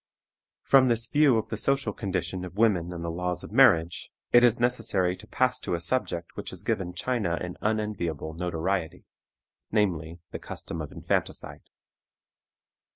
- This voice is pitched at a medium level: No, very low, 95 Hz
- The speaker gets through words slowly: No, average, 155 wpm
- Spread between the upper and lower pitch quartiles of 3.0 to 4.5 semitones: No, average, 5.2 semitones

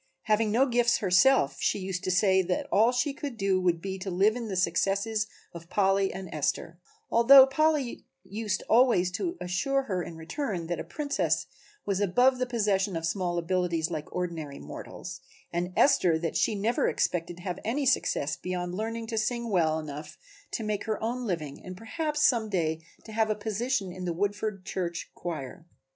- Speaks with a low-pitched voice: No, high, 195 Hz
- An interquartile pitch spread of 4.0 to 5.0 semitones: Yes, average, 4.6 semitones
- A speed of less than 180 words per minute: No, average, 185 wpm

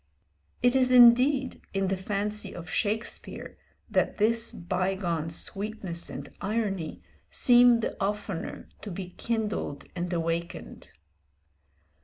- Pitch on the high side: Yes, high, 205 Hz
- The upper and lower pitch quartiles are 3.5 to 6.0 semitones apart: Yes, average, 4.6 semitones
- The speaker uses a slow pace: Yes, slow, 110 wpm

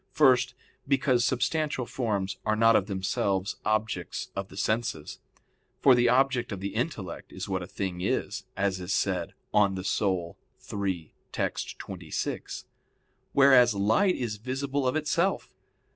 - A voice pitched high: No, low, 110 Hz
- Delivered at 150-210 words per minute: No, average, 140 wpm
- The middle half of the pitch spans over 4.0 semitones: Yes, average, 5.1 semitones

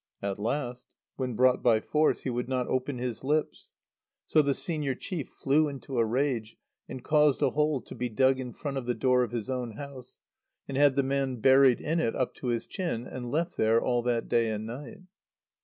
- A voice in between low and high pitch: No, low, 130 Hz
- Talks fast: Yes, fast, 210 wpm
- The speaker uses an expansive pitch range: No, average, 2.8 semitones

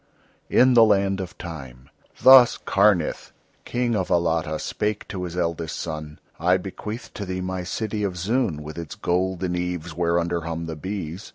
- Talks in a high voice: No, very low, 90 Hz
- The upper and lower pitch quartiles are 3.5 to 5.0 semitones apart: No, average, 3.1 semitones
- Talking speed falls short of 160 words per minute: No, average, 165 wpm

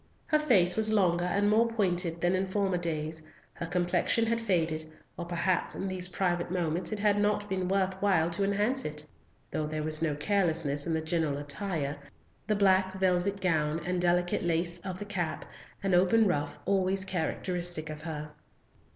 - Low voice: No, medium, 180 Hz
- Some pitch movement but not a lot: Yes, average, 3.3 semitones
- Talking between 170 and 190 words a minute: Yes, average, 175 wpm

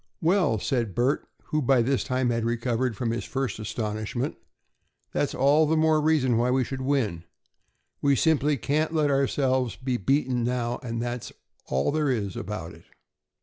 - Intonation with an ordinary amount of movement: Yes, average, 3.4 semitones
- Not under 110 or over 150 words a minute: No, average, 160 wpm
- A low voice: Yes, low, 125 Hz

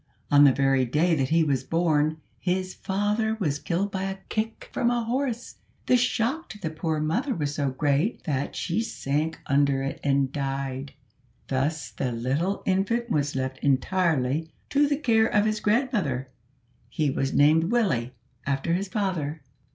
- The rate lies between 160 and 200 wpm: Yes, average, 165 wpm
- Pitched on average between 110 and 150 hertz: No, medium, 160 Hz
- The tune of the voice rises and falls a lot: Yes, wide, 7.1 semitones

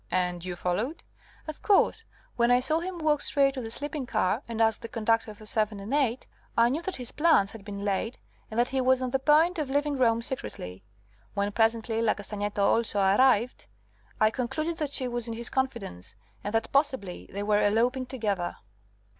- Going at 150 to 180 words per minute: No, average, 195 wpm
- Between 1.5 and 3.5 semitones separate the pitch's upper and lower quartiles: No, average, 4.5 semitones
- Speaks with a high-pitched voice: Yes, high, 235 Hz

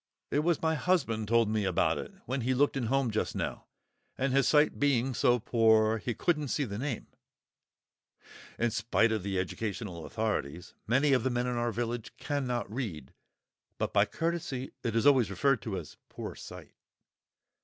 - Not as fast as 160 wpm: No, average, 175 wpm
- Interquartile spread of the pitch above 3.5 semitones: Yes, average, 4.0 semitones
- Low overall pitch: Yes, low, 120 Hz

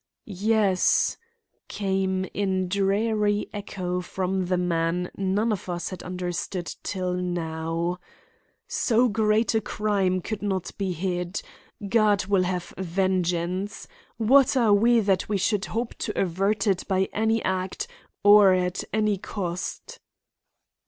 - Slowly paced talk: Yes, slow, 125 wpm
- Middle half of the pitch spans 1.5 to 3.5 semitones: Yes, narrow, 2.5 semitones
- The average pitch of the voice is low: No, high, 190 Hz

